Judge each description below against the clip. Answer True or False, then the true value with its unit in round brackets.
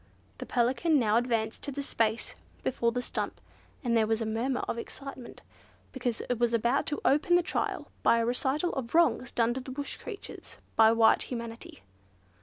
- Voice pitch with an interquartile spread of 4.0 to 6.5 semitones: False (3.0 semitones)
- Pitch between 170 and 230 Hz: False (240 Hz)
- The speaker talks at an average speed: True (185 wpm)